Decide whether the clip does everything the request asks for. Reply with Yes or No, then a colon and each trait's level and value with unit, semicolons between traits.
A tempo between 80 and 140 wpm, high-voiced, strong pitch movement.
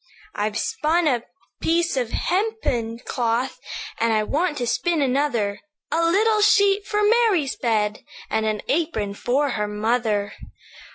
Yes: slow, 135 wpm; very high, 260 Hz; wide, 7.7 semitones